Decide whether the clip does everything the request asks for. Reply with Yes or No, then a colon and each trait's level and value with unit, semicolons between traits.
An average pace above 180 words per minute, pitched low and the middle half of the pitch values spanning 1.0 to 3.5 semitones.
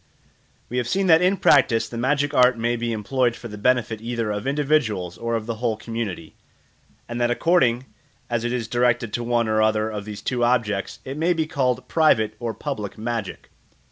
Yes: average, 200 wpm; low, 120 Hz; average, 2.7 semitones